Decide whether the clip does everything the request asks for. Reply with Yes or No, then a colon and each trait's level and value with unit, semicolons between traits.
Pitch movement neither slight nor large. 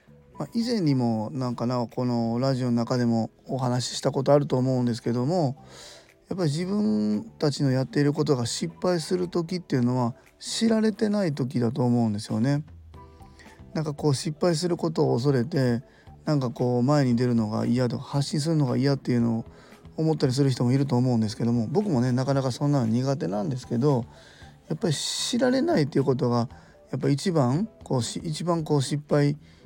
Yes: average, 4.3 semitones